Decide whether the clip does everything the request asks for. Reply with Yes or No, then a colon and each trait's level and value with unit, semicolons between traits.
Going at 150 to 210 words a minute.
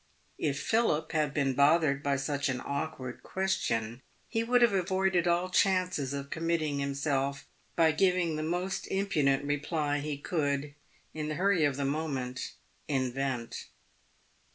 No: average, 140 wpm